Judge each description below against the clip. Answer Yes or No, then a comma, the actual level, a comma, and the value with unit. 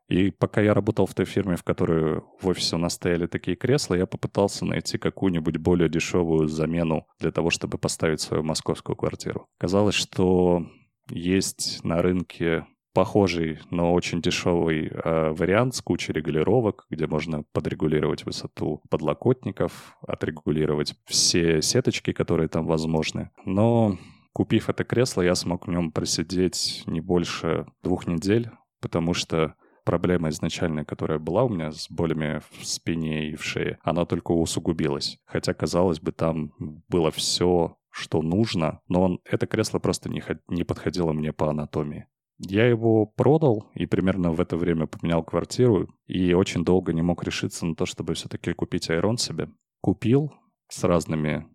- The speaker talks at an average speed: Yes, average, 150 wpm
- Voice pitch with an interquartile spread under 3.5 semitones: Yes, average, 3.0 semitones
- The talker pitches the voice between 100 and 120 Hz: No, very low, 85 Hz